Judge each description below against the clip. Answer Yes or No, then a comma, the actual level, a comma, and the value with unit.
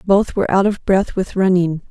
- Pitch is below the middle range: No, high, 190 Hz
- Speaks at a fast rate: Yes, fast, 220 wpm